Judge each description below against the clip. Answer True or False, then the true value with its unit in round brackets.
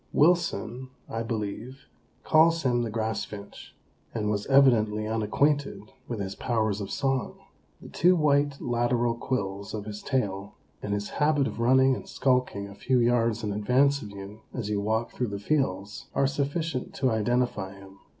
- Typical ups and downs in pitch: True (4.4 semitones)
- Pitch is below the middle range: True (115 Hz)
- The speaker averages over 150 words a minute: True (165 wpm)